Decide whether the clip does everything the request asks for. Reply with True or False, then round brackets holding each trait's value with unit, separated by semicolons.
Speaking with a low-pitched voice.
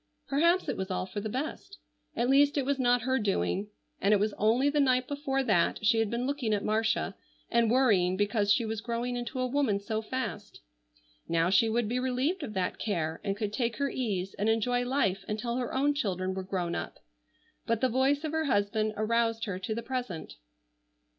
False (230 Hz)